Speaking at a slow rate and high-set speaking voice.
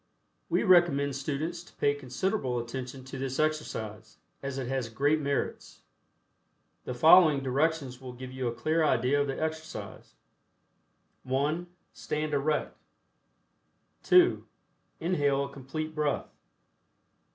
No: slow, 120 wpm; medium, 140 Hz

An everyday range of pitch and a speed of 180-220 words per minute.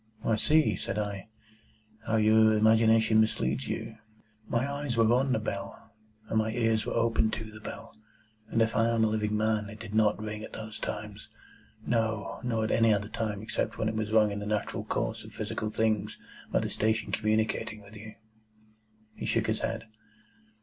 No: narrow, 0.9 semitones; average, 190 wpm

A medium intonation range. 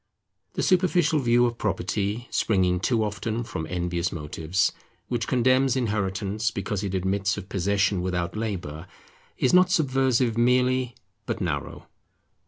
Yes: average, 4.9 semitones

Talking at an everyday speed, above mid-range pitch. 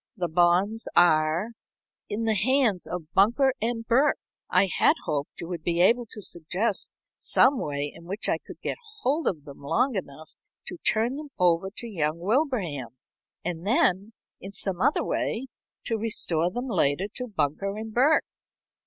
Yes: average, 170 wpm; high, 195 Hz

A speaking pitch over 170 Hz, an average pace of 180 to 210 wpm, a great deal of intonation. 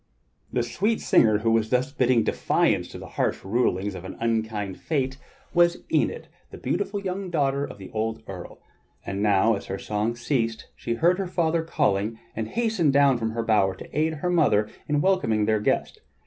No: low, 115 Hz; average, 190 wpm; wide, 6.7 semitones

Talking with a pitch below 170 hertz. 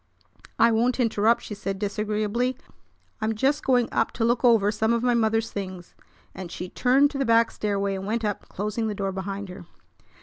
No: high, 220 Hz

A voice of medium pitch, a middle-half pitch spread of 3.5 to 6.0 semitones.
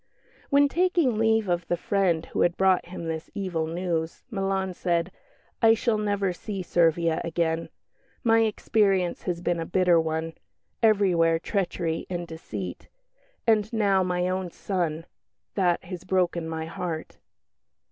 No: medium, 180 Hz; average, 3.1 semitones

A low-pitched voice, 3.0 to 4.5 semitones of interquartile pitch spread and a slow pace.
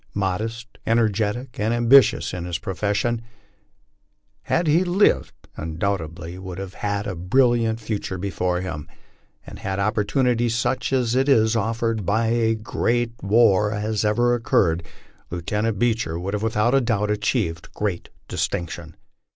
No: low, 110 Hz; average, 3.6 semitones; average, 150 wpm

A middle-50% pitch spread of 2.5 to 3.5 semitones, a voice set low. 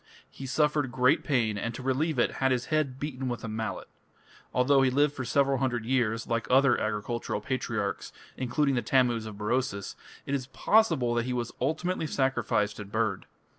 Yes: average, 3.0 semitones; low, 125 Hz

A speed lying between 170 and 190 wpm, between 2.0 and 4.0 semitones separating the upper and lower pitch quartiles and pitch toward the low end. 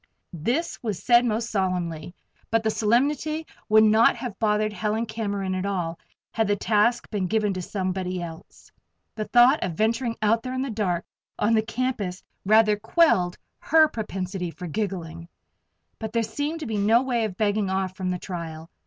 No: average, 175 wpm; average, 3.7 semitones; high, 210 Hz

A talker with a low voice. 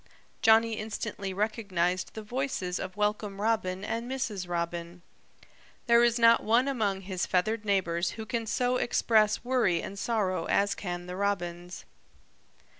No: high, 205 Hz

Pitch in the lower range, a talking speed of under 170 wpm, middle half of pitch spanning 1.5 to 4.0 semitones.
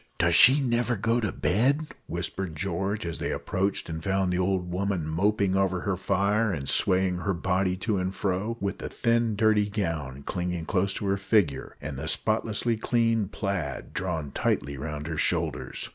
No: very low, 95 Hz; average, 175 wpm; average, 3.6 semitones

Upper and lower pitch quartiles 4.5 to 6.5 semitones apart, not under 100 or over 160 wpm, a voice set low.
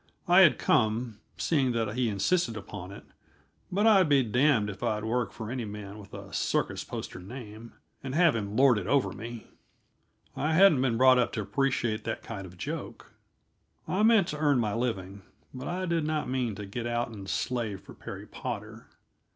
No: average, 5.0 semitones; average, 190 wpm; low, 120 Hz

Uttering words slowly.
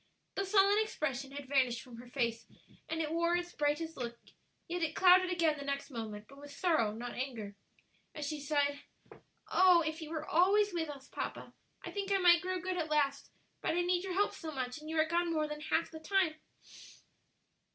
No: fast, 205 wpm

